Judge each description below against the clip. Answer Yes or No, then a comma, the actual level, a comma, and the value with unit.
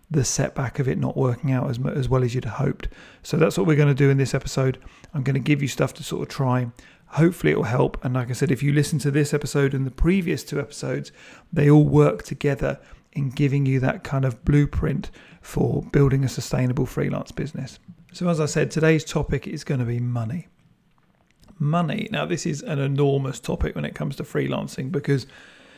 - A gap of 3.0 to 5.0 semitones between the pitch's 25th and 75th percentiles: No, narrow, 2.6 semitones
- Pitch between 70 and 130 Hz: No, medium, 140 Hz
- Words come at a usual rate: No, fast, 215 wpm